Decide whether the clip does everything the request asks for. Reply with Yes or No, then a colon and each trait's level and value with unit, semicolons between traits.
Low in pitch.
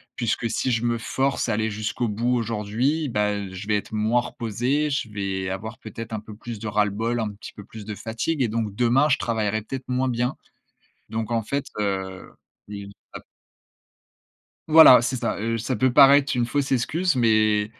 Yes: low, 115 Hz